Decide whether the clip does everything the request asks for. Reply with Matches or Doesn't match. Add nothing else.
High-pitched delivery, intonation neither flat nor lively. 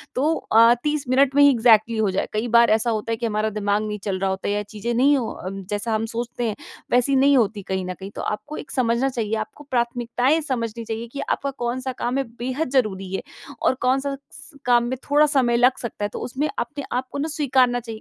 Matches